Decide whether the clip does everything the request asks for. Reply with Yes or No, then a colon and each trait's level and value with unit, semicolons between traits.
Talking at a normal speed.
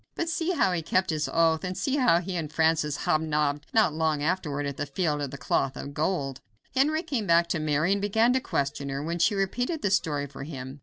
No: fast, 235 wpm